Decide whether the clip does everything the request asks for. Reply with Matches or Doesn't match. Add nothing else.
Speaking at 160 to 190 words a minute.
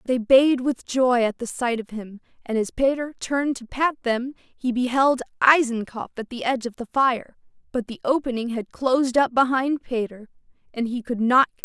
Doesn't match